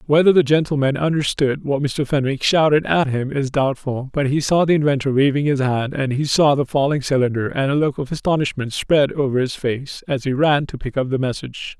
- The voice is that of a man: Yes, male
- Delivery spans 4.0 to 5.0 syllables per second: No, 5.5 syllables/s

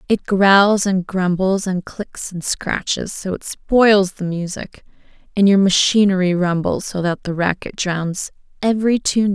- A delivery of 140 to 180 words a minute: Yes, average, 165 wpm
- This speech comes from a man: No, female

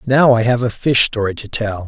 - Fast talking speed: Yes, fast, 255 wpm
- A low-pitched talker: Yes, low, 115 Hz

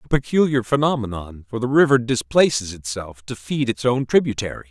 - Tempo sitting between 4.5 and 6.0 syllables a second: Yes, 5.5 syllables/s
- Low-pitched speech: Yes, low, 120 Hz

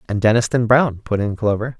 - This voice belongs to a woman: No, male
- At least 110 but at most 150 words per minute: No, average, 200 wpm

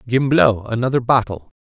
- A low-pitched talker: Yes, low, 115 Hz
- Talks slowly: Yes, slow, 110 wpm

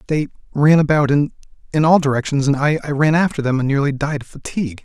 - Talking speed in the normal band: Yes, average, 175 wpm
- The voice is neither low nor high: Yes, medium, 145 Hz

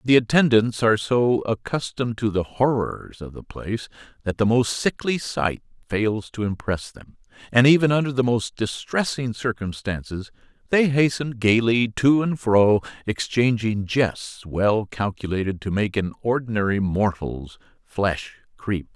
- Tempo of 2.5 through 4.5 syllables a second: Yes, 4.4 syllables/s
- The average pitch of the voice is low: Yes, low, 110 Hz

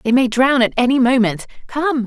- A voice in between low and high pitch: No, high, 245 Hz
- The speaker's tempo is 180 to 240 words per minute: Yes, fast, 205 wpm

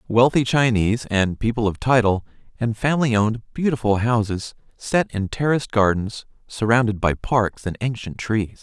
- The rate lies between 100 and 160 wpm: Yes, average, 145 wpm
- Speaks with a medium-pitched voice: No, low, 115 Hz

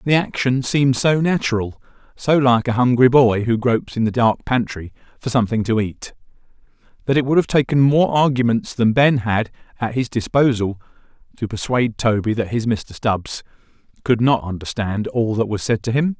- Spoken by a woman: No, male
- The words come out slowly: No, average, 180 wpm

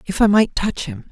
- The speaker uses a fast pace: Yes, fast, 270 wpm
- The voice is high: Yes, high, 200 Hz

